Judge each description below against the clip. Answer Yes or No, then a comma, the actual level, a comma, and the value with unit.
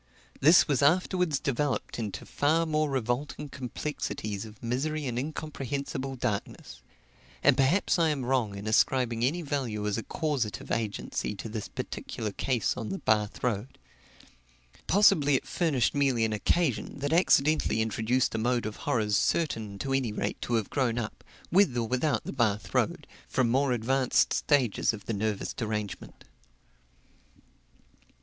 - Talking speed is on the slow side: No, average, 150 wpm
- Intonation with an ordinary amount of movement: Yes, average, 4.6 semitones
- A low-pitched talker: Yes, low, 125 Hz